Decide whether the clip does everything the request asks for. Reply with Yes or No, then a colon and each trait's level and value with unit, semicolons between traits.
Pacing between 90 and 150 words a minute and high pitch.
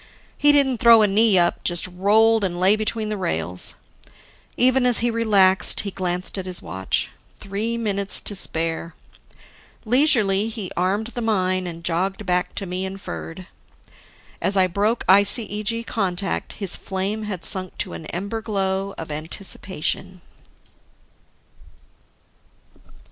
Yes: average, 140 wpm; high, 195 Hz